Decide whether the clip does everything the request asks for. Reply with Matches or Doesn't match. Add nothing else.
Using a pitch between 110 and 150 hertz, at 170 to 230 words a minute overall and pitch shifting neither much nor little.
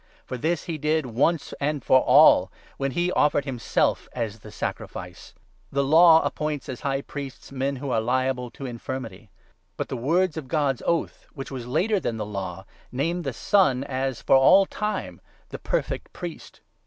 Matches